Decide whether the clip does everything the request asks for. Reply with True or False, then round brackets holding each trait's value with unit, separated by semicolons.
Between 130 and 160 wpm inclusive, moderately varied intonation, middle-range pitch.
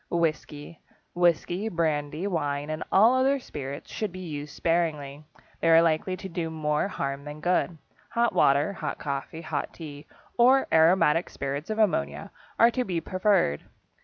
True (155 wpm; 4.1 semitones; 165 Hz)